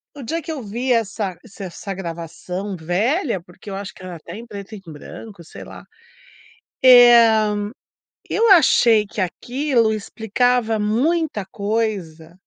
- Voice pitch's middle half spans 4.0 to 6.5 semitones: Yes, average, 4.3 semitones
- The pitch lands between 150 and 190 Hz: No, high, 215 Hz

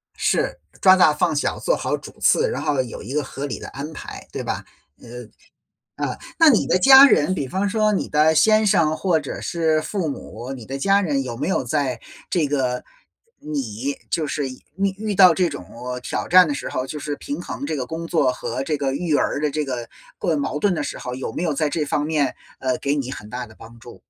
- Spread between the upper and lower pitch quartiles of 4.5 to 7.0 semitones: Yes, average, 5.2 semitones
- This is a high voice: No, medium, 150 Hz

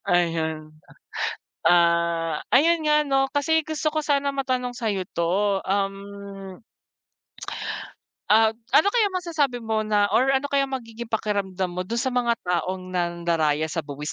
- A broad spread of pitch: Yes, wide, 7.4 semitones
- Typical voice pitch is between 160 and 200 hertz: No, high, 210 Hz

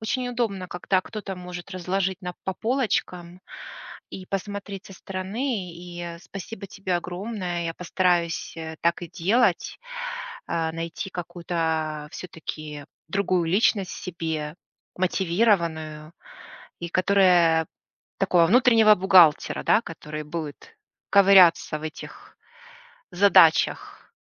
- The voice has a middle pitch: Yes, medium, 180 Hz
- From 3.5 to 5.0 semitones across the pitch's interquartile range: No, average, 3.0 semitones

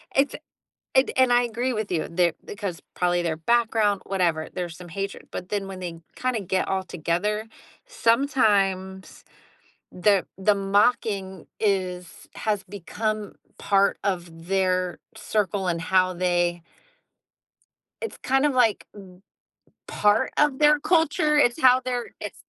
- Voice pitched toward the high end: Yes, high, 195 Hz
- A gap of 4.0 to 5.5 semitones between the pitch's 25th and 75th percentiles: Yes, average, 4.4 semitones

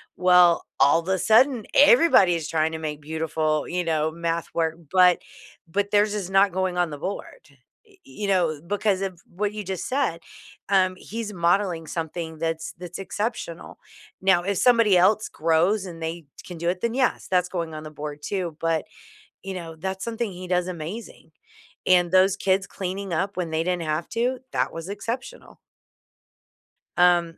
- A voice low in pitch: No, medium, 180 Hz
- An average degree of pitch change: Yes, average, 3.3 semitones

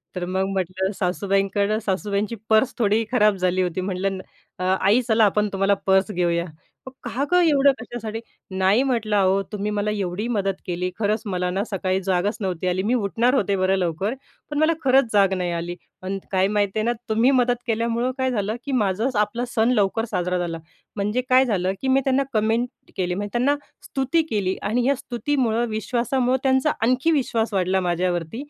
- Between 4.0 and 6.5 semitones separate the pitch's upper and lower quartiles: Yes, average, 4.3 semitones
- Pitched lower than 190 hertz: No, high, 210 Hz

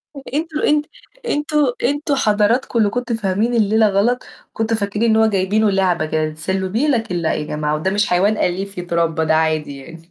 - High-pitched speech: Yes, high, 200 Hz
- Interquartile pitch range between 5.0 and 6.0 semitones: Yes, average, 5.3 semitones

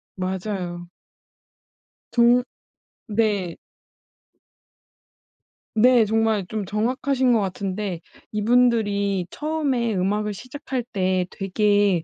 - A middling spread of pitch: Yes, average, 3.7 semitones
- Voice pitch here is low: No, high, 210 Hz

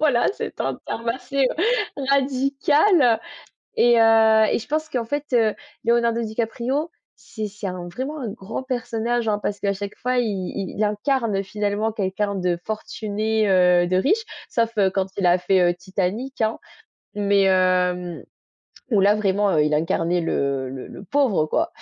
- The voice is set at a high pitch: Yes, high, 215 Hz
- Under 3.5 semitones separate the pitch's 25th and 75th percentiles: No, average, 4.3 semitones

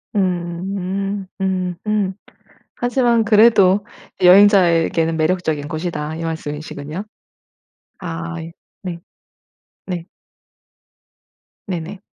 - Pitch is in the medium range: Yes, medium, 180 Hz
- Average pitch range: Yes, average, 3.2 semitones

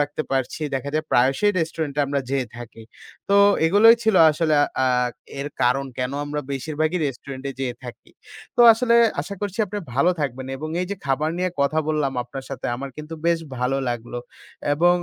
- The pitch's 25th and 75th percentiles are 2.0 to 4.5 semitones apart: Yes, average, 3.9 semitones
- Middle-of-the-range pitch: Yes, medium, 145 Hz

